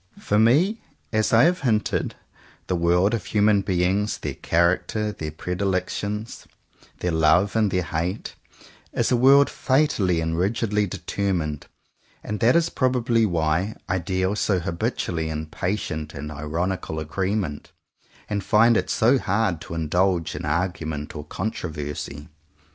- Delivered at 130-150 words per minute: Yes, average, 140 wpm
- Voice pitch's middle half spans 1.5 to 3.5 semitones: No, average, 4.7 semitones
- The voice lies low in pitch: Yes, very low, 95 Hz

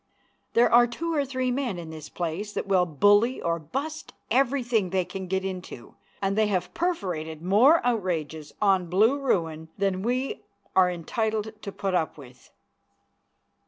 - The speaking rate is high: No, average, 160 wpm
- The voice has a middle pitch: No, high, 195 Hz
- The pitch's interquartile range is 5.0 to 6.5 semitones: Yes, wide, 5.6 semitones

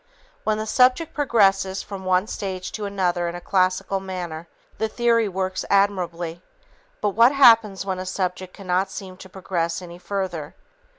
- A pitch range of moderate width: No, narrow, 2.1 semitones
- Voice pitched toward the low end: No, high, 190 Hz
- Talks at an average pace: Yes, average, 160 wpm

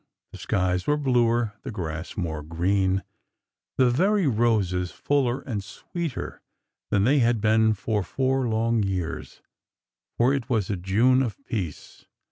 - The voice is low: Yes, low, 110 Hz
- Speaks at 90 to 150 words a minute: Yes, average, 140 wpm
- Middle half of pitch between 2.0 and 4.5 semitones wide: No, average, 5.1 semitones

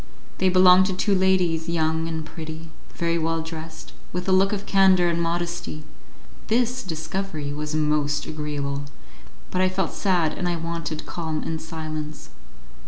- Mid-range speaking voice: Yes, medium, 165 Hz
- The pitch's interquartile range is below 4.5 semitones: Yes, average, 2.8 semitones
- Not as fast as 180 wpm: Yes, average, 155 wpm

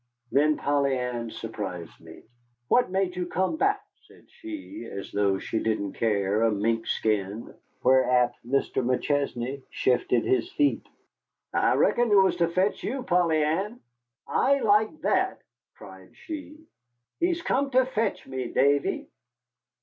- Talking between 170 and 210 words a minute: No, slow, 135 wpm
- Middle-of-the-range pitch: Yes, medium, 145 Hz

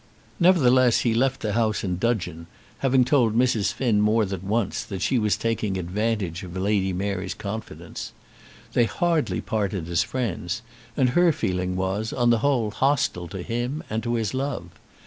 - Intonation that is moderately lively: Yes, average, 4.5 semitones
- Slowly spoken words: No, average, 165 wpm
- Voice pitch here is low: Yes, low, 110 Hz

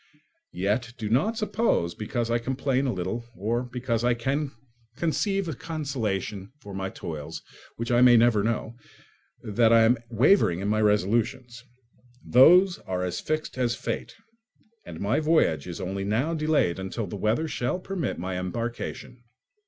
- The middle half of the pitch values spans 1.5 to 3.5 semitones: No, average, 4.9 semitones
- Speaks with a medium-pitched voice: No, low, 115 Hz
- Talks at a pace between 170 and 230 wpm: No, average, 155 wpm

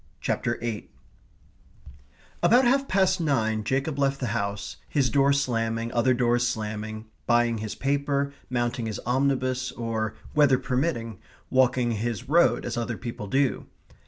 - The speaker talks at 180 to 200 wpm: No, slow, 135 wpm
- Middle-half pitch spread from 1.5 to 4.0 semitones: Yes, average, 3.4 semitones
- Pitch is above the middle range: No, low, 120 Hz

